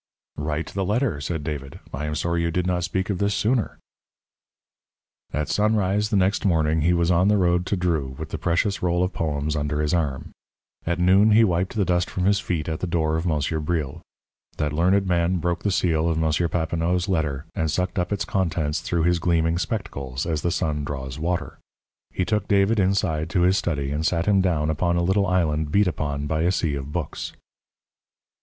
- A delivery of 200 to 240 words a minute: Yes, fast, 205 wpm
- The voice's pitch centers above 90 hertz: No, very low, 85 Hz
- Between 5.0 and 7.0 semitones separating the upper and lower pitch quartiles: No, average, 3.2 semitones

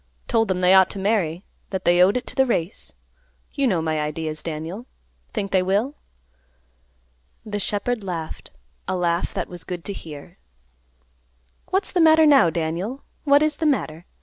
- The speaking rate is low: No, average, 170 wpm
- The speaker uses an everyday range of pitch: No, wide, 6.6 semitones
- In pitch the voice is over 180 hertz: Yes, high, 190 Hz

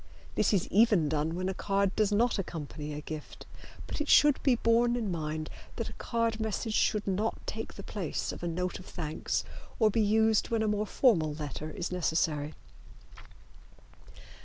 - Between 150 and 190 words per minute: Yes, average, 180 wpm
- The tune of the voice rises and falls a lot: Yes, wide, 5.7 semitones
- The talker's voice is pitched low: No, high, 195 Hz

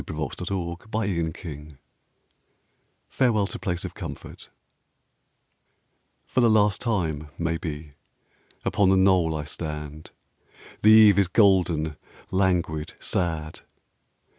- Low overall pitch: Yes, very low, 85 Hz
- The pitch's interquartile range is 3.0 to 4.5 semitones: Yes, average, 4.2 semitones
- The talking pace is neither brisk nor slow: No, slow, 110 wpm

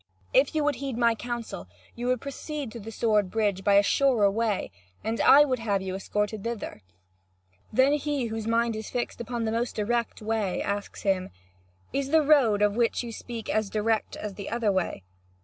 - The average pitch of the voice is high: Yes, high, 225 Hz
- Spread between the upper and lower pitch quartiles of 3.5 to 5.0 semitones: No, average, 2.9 semitones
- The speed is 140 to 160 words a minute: No, average, 195 wpm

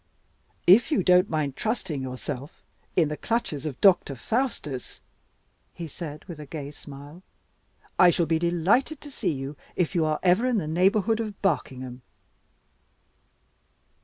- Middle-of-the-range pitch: Yes, medium, 170 Hz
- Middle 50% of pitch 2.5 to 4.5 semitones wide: No, average, 5.3 semitones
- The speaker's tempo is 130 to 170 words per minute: Yes, average, 145 wpm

